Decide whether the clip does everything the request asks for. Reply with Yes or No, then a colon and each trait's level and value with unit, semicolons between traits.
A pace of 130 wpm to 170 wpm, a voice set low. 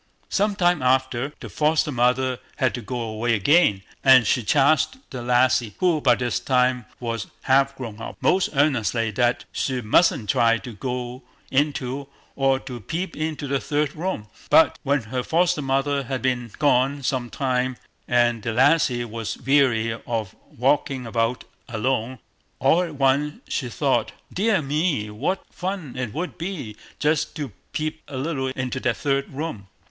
Yes: average, 160 wpm; low, 130 Hz